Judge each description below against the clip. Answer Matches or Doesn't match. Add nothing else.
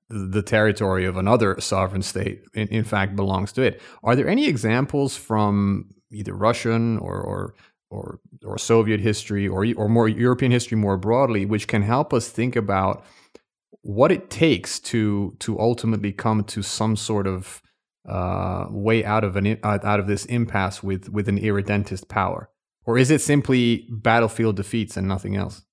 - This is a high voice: Doesn't match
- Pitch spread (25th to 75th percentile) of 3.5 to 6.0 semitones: Doesn't match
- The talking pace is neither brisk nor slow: Matches